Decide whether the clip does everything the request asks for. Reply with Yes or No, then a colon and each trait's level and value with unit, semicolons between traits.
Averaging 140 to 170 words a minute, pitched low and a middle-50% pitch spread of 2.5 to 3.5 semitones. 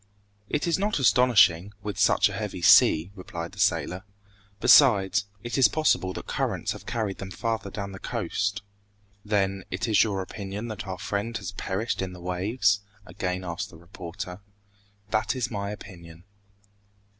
Yes: average, 160 wpm; low, 100 Hz; average, 2.9 semitones